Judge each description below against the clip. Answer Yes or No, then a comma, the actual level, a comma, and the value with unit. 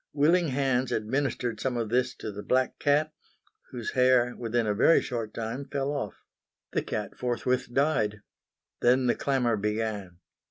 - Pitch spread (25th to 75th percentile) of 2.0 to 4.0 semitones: Yes, average, 3.3 semitones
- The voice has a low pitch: Yes, low, 125 Hz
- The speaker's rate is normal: Yes, average, 155 wpm